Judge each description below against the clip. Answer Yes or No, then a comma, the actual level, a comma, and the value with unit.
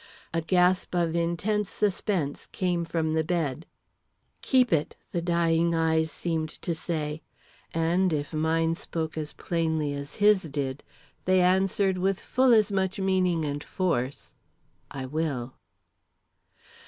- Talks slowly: Yes, slow, 130 wpm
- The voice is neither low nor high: Yes, medium, 165 Hz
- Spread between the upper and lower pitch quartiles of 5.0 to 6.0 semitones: No, average, 2.9 semitones